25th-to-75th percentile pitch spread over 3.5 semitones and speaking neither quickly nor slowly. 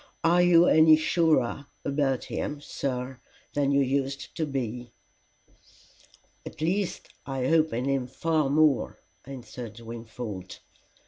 No: average, 3.9 semitones; slow, 120 wpm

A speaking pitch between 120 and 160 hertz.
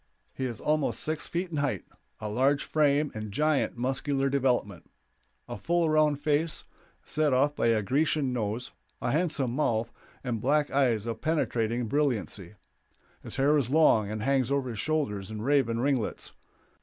Yes: low, 135 Hz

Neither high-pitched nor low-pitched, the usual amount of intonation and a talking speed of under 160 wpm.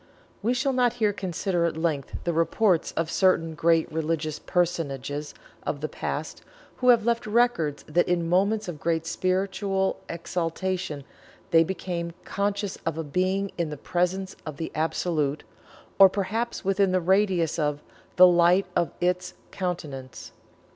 Yes: medium, 175 Hz; average, 3.1 semitones; average, 145 wpm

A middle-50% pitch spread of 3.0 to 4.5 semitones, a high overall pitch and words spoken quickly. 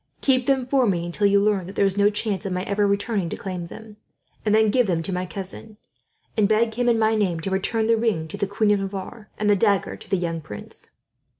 No: narrow, 2.6 semitones; high, 205 Hz; fast, 255 wpm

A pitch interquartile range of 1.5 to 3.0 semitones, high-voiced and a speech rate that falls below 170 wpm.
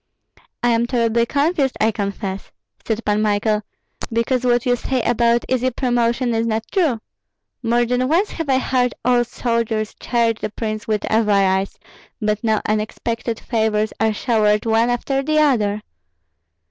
Yes: narrow, 2.5 semitones; high, 230 Hz; average, 150 wpm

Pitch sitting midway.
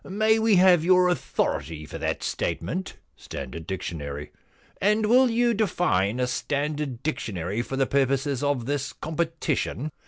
Yes: medium, 145 Hz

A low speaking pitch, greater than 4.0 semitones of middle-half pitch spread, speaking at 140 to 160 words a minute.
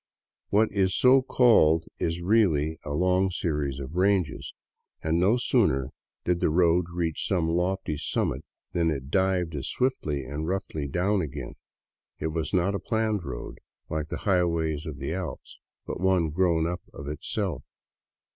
No: very low, 85 Hz; average, 3.7 semitones; average, 155 wpm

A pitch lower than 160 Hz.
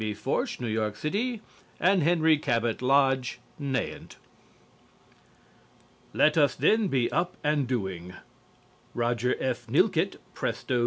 Yes: low, 135 Hz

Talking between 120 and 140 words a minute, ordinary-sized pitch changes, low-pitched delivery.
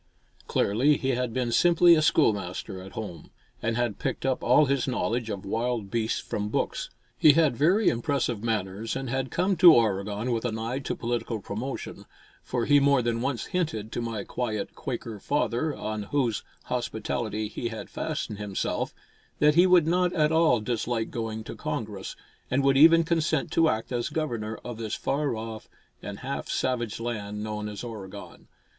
No: average, 175 wpm; average, 4.4 semitones; low, 120 Hz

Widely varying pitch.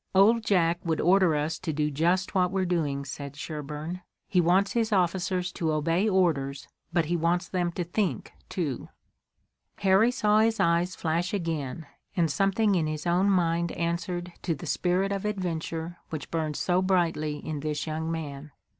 No: average, 3.1 semitones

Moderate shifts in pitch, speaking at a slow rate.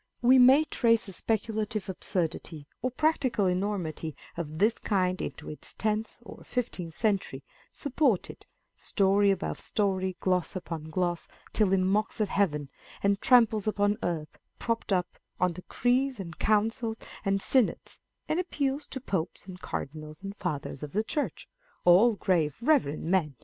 No: average, 4.3 semitones; average, 150 wpm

